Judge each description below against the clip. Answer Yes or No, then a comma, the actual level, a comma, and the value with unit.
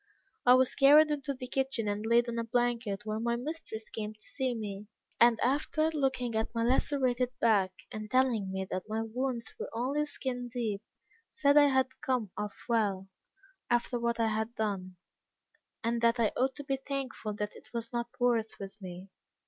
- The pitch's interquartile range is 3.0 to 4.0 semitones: Yes, average, 3.3 semitones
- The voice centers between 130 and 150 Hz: No, high, 235 Hz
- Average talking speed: Yes, average, 185 wpm